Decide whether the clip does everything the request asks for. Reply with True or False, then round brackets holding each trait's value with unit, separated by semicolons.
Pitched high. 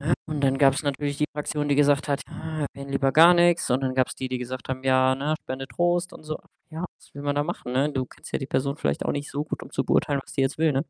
False (140 Hz)